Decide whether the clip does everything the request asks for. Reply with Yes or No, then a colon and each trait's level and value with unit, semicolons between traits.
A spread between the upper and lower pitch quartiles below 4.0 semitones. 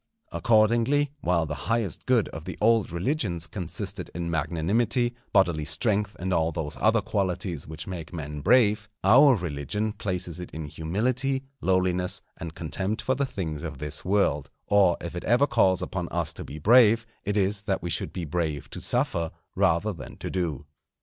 No: average, 4.9 semitones